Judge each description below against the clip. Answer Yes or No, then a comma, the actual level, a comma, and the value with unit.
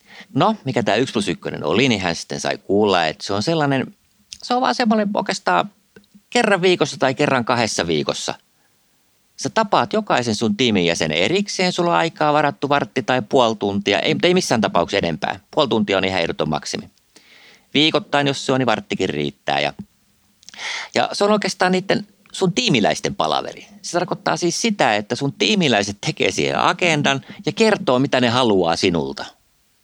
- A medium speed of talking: No, fast, 170 wpm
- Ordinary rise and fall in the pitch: No, wide, 8.7 semitones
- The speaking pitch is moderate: Yes, medium, 145 Hz